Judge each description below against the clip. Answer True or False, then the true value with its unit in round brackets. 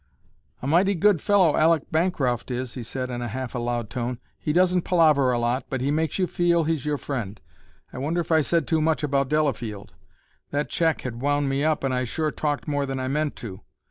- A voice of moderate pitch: True (145 Hz)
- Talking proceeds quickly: True (220 wpm)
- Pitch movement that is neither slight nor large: True (4.1 semitones)